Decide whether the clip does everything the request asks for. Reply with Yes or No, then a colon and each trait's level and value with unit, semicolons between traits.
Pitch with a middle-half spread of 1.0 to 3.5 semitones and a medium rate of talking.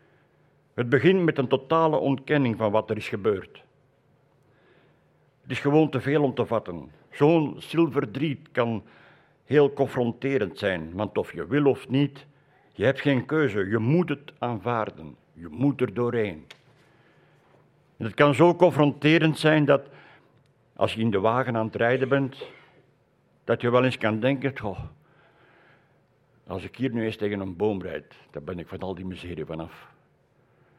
No: average, 4.3 semitones; average, 160 wpm